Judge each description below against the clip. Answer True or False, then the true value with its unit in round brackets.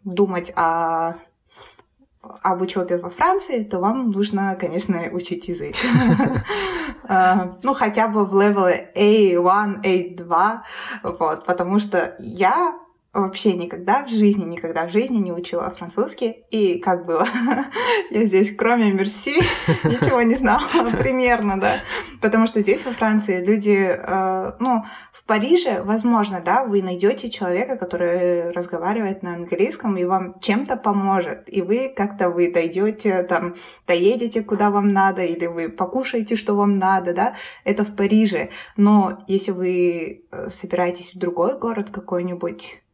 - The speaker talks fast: False (135 wpm)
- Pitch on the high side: True (195 Hz)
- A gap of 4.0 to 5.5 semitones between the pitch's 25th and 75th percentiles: False (3.6 semitones)